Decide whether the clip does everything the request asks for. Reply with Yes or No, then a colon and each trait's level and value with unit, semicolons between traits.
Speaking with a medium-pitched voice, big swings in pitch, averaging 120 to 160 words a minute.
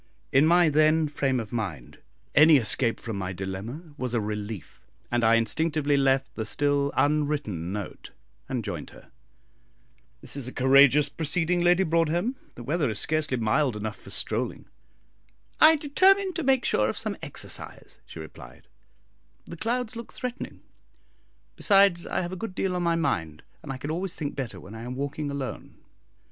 No: medium, 145 Hz; wide, 7.0 semitones; average, 170 wpm